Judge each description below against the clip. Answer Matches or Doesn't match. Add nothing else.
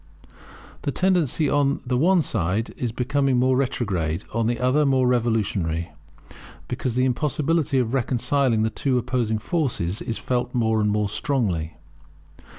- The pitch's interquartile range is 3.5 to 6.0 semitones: Matches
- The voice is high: Doesn't match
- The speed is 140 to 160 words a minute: Matches